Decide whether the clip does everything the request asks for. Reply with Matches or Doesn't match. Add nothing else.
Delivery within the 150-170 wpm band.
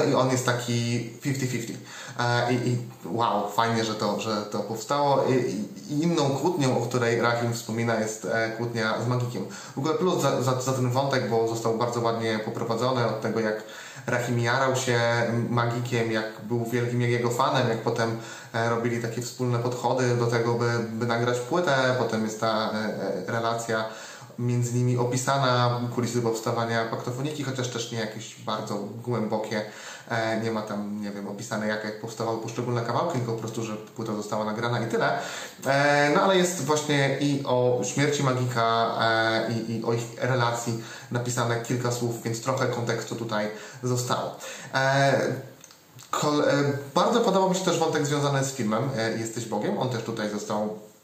Matches